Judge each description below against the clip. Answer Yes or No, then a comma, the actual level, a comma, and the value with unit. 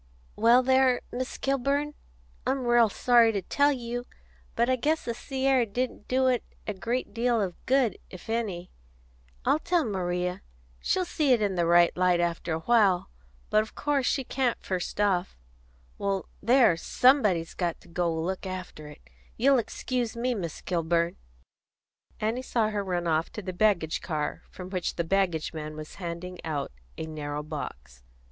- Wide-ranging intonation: Yes, wide, 6.2 semitones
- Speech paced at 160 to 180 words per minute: Yes, average, 165 wpm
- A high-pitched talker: Yes, high, 205 Hz